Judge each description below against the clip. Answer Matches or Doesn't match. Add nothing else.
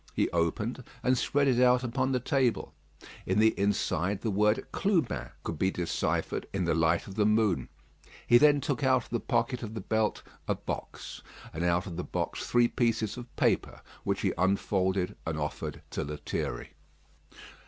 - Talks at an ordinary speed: Matches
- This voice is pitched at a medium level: Doesn't match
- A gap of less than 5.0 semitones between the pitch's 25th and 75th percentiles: Doesn't match